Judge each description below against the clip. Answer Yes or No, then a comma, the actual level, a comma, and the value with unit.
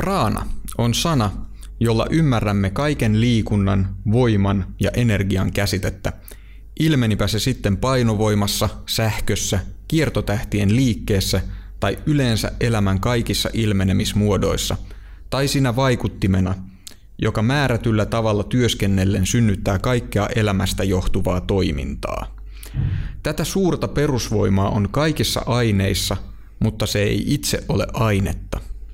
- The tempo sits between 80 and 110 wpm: Yes, slow, 95 wpm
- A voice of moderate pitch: No, low, 105 Hz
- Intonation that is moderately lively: Yes, average, 3.4 semitones